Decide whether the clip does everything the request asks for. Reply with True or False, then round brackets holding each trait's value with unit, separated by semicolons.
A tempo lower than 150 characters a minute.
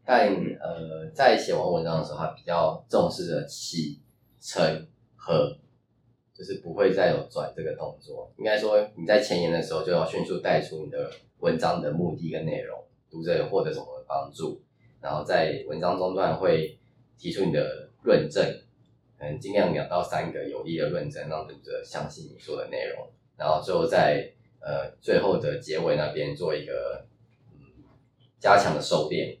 False (250 characters per minute)